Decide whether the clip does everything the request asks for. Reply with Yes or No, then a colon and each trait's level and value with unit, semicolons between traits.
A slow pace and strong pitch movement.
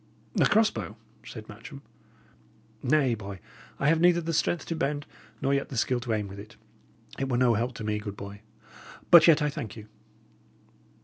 No: average, 190 wpm; wide, 5.8 semitones